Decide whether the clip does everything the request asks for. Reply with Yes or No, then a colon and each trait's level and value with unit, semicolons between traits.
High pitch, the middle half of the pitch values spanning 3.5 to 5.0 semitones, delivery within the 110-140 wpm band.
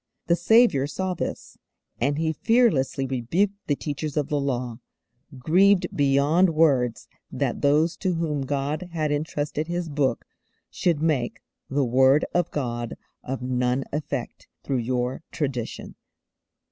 No: medium, 145 Hz; average, 3.8 semitones; slow, 135 wpm